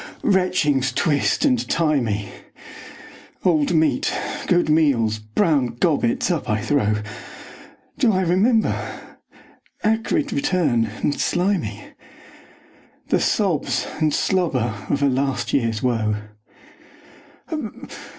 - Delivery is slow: Yes, slow, 100 wpm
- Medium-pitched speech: Yes, medium, 150 Hz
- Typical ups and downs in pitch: No, wide, 7.5 semitones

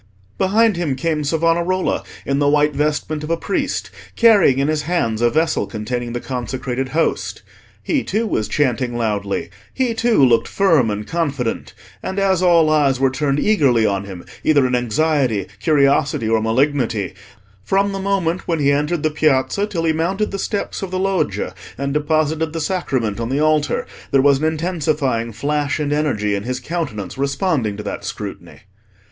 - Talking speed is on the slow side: No, average, 175 wpm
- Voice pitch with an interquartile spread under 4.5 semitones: No, average, 5.1 semitones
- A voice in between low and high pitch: Yes, medium, 145 Hz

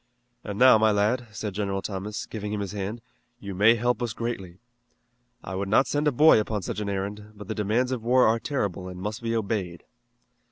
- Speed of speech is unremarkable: No, fast, 210 wpm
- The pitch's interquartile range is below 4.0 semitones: Yes, average, 2.8 semitones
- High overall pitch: No, low, 105 Hz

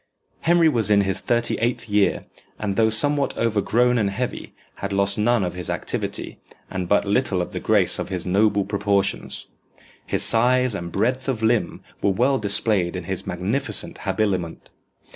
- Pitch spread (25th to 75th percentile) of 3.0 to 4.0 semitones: Yes, average, 3.6 semitones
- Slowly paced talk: No, average, 165 wpm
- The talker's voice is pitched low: Yes, low, 105 Hz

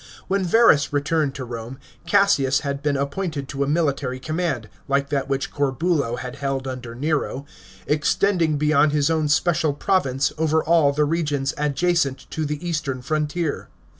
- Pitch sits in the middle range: Yes, medium, 145 Hz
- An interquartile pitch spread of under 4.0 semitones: Yes, average, 2.8 semitones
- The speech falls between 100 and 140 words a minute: No, average, 165 wpm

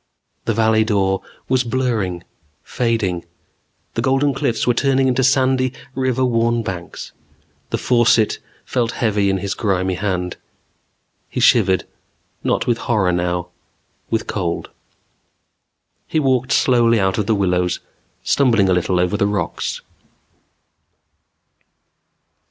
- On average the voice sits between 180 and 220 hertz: No, low, 110 Hz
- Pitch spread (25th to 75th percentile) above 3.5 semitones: Yes, average, 4.7 semitones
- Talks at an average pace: No, slow, 120 wpm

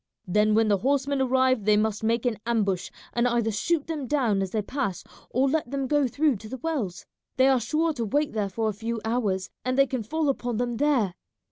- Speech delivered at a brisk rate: Yes, fast, 225 wpm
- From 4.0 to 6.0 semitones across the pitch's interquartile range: Yes, average, 4.3 semitones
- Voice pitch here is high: Yes, high, 240 Hz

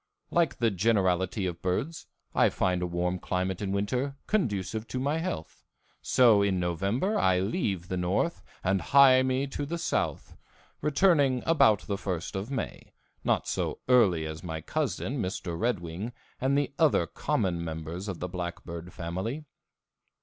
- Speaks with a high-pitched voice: No, low, 100 Hz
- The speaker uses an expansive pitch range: Yes, wide, 6.6 semitones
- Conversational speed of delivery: Yes, average, 155 wpm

